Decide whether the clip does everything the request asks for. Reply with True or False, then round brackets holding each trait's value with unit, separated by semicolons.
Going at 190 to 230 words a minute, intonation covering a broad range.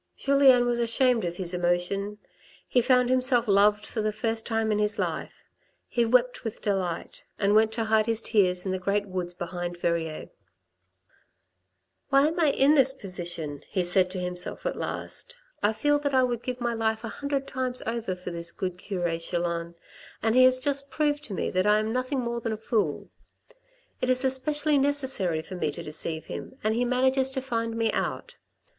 True (200 wpm; 5.9 semitones)